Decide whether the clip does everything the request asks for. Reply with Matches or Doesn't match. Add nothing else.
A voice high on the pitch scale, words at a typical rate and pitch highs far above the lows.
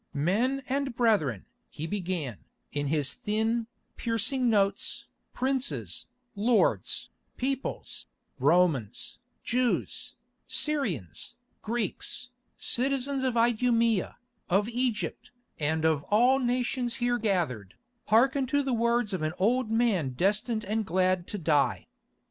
Doesn't match